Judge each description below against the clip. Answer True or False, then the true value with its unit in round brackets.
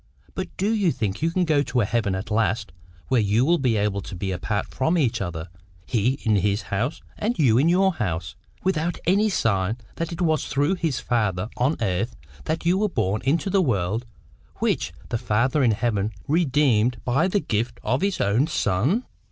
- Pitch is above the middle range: False (120 Hz)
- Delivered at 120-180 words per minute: False (195 wpm)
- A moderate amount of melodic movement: False (7.8 semitones)